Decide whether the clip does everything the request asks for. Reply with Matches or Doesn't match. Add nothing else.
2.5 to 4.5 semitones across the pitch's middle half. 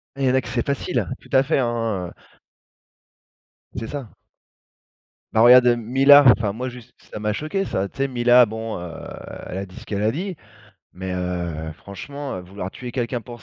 Doesn't match